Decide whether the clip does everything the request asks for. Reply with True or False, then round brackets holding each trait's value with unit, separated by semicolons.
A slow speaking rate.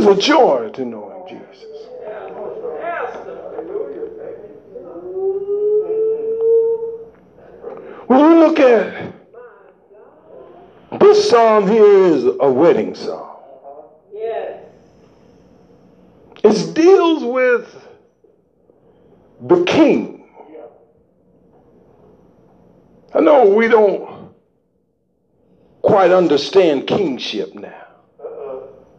True (65 wpm)